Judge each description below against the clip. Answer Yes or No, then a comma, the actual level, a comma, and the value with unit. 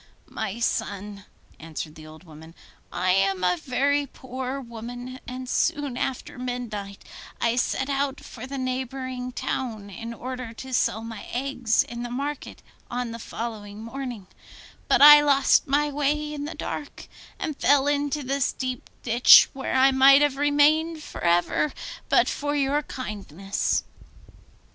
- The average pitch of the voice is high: Yes, very high, 255 Hz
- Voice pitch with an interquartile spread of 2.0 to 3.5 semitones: No, average, 3.9 semitones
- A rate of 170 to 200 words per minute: No, average, 150 wpm